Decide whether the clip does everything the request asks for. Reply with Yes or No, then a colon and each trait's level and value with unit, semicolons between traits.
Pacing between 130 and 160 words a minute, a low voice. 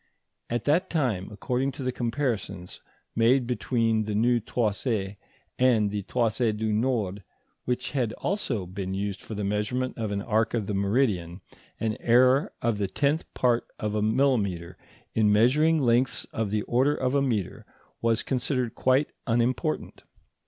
Yes: average, 155 wpm; low, 115 Hz